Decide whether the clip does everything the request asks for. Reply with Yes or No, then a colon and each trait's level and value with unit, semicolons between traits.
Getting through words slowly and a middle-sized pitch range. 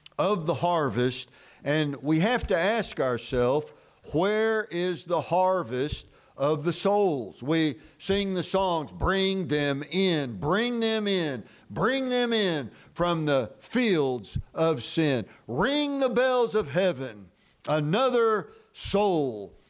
No: slow, 125 wpm; wide, 6.5 semitones